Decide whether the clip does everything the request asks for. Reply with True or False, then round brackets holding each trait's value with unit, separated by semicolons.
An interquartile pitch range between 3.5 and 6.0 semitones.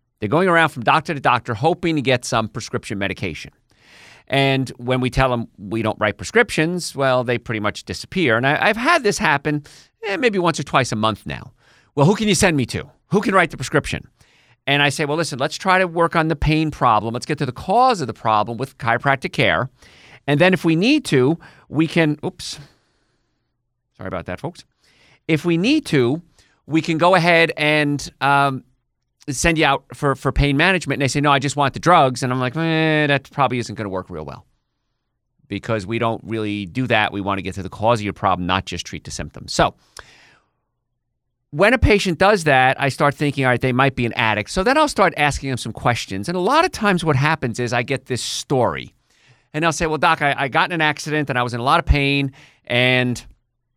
True (5.0 semitones)